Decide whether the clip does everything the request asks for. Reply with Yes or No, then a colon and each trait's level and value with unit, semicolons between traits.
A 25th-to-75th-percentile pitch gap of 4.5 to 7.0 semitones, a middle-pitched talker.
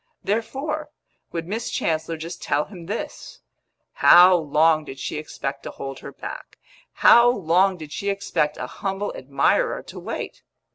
Yes: average, 4.9 semitones; medium, 170 Hz